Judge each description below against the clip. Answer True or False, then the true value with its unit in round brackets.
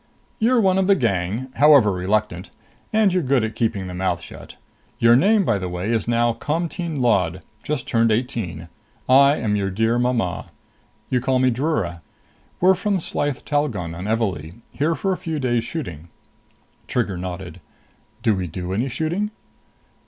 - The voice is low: True (120 Hz)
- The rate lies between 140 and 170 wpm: True (165 wpm)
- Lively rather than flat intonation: True (8.0 semitones)